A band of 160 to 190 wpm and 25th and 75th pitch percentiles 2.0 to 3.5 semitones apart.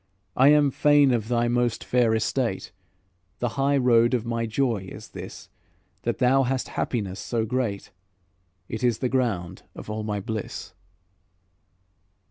No: average, 145 wpm; average, 2.9 semitones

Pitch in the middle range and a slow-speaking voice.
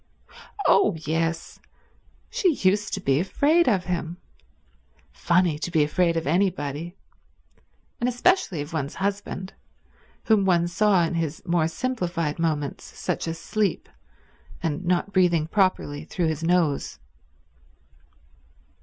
Yes: medium, 175 Hz; slow, 120 wpm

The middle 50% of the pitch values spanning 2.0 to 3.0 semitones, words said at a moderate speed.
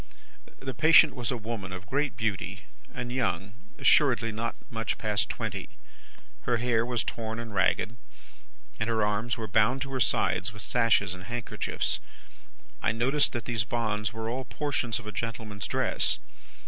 Yes: narrow, 2.4 semitones; average, 160 wpm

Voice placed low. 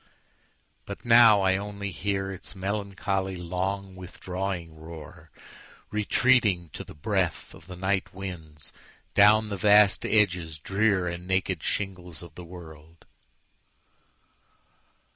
Yes: very low, 95 Hz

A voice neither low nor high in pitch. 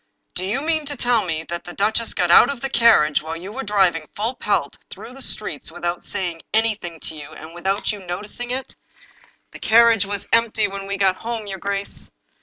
No: high, 200 Hz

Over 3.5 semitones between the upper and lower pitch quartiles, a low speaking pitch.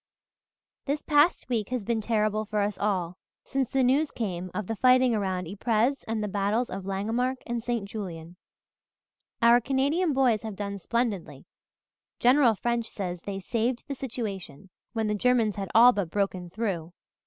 No: average, 3.9 semitones; high, 220 Hz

